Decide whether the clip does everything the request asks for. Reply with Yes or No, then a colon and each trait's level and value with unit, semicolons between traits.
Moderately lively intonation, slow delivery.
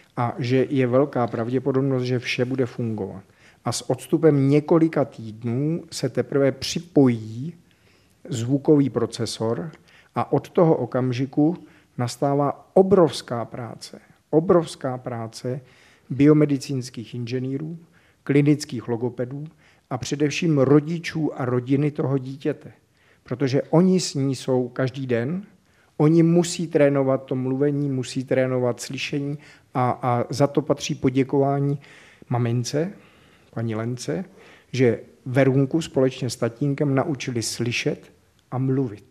Yes: average, 3.3 semitones; slow, 110 wpm